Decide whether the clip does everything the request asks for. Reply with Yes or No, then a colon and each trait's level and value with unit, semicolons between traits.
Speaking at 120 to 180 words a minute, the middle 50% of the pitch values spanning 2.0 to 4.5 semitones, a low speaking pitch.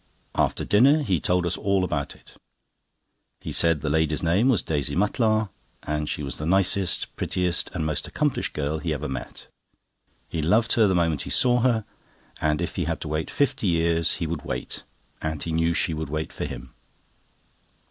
No: average, 190 wpm; average, 4.2 semitones; very low, 85 Hz